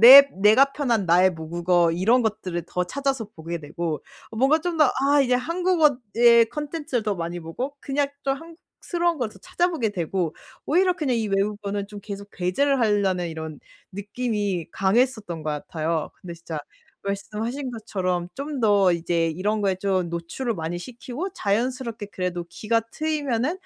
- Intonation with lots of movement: Yes, wide, 7.1 semitones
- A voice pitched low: No, high, 210 Hz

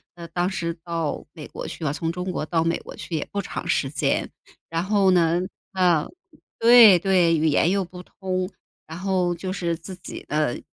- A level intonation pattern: Yes, narrow, 2.3 semitones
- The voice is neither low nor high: Yes, medium, 175 Hz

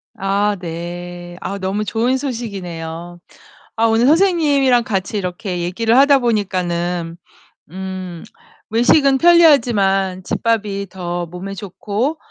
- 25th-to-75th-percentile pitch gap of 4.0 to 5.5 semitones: Yes, average, 5.1 semitones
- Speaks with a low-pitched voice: No, high, 200 Hz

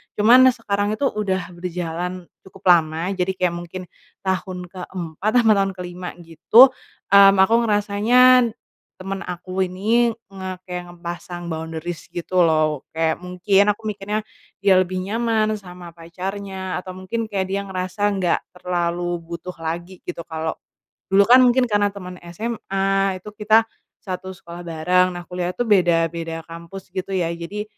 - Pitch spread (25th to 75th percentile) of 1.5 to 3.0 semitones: Yes, narrow, 2.6 semitones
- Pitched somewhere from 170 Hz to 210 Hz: Yes, medium, 185 Hz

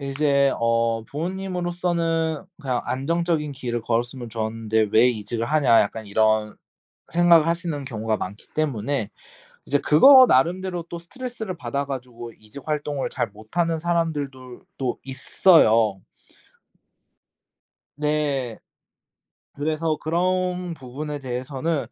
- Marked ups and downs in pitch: Yes, wide, 5.9 semitones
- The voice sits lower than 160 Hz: Yes, medium, 140 Hz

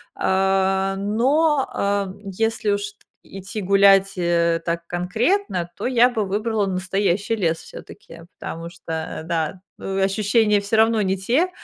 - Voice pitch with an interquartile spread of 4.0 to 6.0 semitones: No, average, 3.0 semitones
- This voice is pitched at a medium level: No, high, 195 Hz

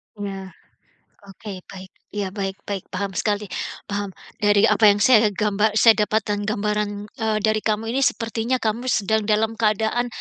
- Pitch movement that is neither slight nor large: No, narrow, 1.5 semitones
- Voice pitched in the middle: No, high, 210 Hz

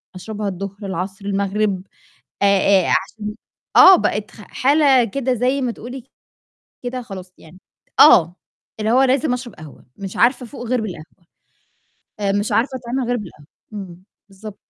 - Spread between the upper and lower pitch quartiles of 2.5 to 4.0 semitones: No, average, 4.4 semitones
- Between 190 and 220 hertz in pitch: Yes, high, 210 Hz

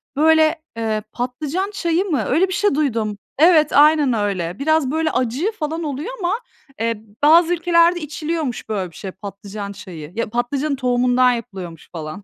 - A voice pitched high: Yes, very high, 275 Hz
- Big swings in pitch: Yes, wide, 6.9 semitones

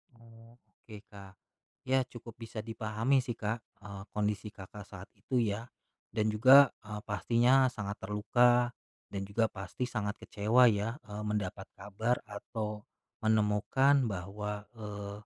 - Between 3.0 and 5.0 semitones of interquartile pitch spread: No, narrow, 2.6 semitones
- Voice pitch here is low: Yes, low, 105 Hz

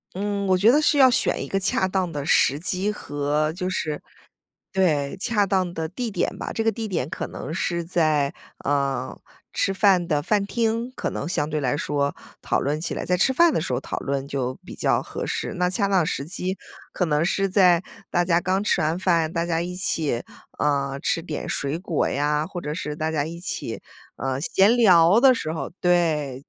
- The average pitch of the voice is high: No, medium, 170 Hz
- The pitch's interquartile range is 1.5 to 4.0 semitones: No, average, 4.4 semitones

